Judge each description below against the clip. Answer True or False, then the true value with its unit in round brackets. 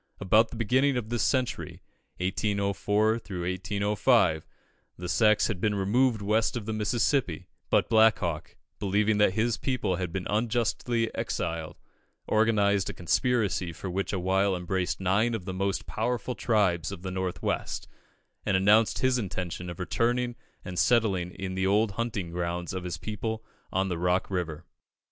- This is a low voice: True (100 Hz)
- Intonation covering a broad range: False (3.6 semitones)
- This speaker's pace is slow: False (160 wpm)